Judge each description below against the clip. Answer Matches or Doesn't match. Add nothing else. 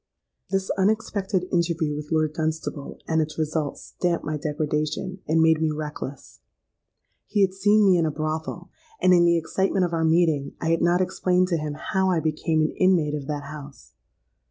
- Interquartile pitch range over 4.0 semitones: Doesn't match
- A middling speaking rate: Matches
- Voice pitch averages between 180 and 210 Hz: Doesn't match